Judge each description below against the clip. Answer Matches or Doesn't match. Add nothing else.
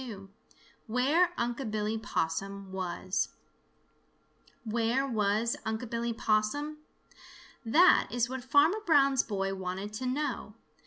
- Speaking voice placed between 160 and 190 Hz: Doesn't match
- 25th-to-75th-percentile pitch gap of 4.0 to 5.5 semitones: Matches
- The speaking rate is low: Matches